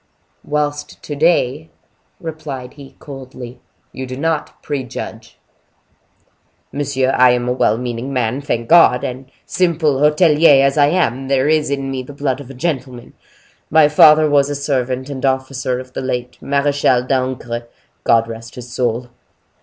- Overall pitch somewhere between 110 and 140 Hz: Yes, low, 135 Hz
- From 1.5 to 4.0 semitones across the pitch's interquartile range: Yes, narrow, 2.6 semitones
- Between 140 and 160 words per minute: Yes, average, 155 wpm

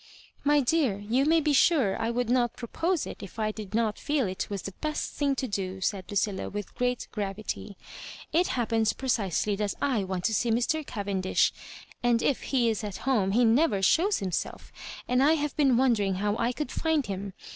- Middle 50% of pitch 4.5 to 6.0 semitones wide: Yes, average, 5.1 semitones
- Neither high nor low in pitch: No, high, 230 Hz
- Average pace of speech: No, fast, 210 wpm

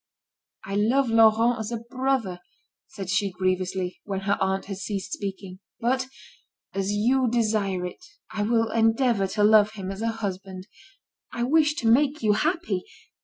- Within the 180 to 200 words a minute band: No, average, 160 wpm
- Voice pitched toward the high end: Yes, high, 215 Hz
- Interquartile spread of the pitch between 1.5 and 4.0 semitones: Yes, average, 3.6 semitones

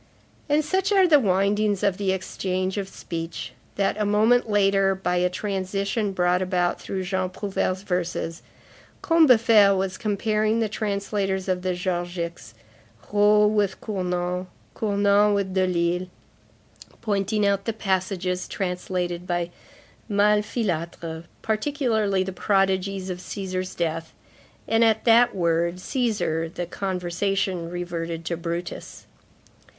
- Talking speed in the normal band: No, slow, 120 wpm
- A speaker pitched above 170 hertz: Yes, high, 190 Hz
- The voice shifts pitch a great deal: No, narrow, 2.6 semitones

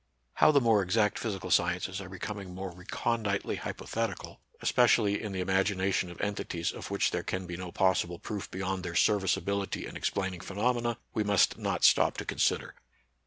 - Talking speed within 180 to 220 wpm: No, average, 170 wpm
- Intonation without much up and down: Yes, narrow, 2.3 semitones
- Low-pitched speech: Yes, very low, 95 Hz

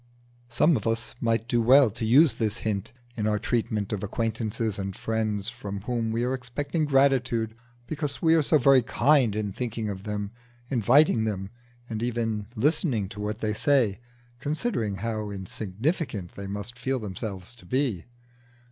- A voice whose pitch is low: Yes, low, 115 Hz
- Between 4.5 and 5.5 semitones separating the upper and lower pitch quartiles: No, average, 3.8 semitones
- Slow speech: No, average, 165 wpm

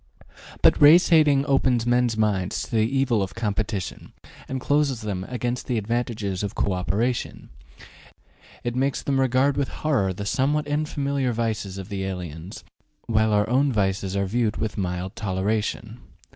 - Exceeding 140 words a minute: Yes, average, 155 wpm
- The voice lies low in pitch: Yes, low, 115 Hz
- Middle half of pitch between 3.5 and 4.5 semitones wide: No, average, 5.0 semitones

